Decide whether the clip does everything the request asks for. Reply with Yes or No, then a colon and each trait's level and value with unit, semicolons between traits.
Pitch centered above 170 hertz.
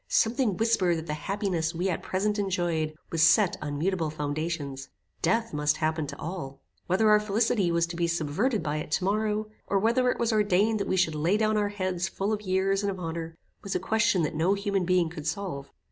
Yes: medium, 185 Hz